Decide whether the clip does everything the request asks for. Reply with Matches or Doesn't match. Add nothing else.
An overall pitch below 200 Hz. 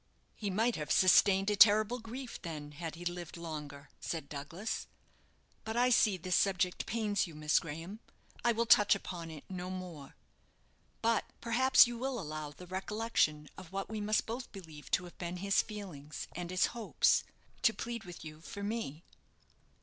Matches